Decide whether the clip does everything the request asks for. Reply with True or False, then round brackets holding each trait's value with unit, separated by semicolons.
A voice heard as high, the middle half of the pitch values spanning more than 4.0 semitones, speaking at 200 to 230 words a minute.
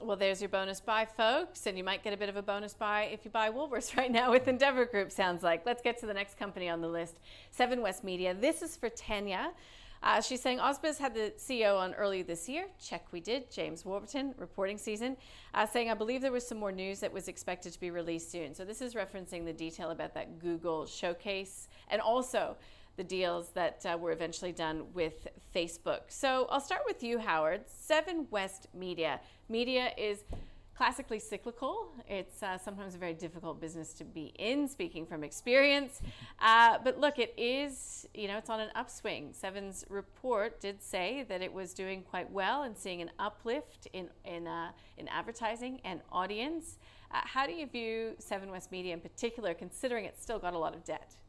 True (205 Hz; 5.0 semitones; 205 wpm)